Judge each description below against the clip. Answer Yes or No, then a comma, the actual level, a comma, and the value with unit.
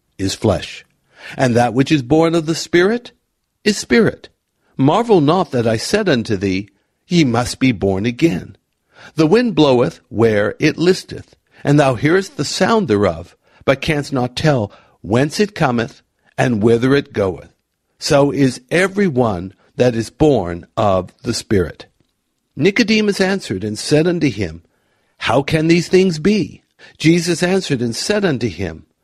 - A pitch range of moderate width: No, wide, 7.6 semitones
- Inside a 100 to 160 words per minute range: Yes, average, 155 wpm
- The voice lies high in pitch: No, low, 135 Hz